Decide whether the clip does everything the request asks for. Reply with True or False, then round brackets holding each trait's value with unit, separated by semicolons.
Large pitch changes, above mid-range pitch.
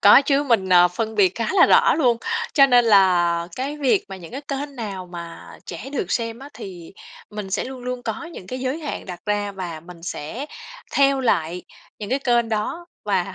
True (6.5 semitones; 220 Hz)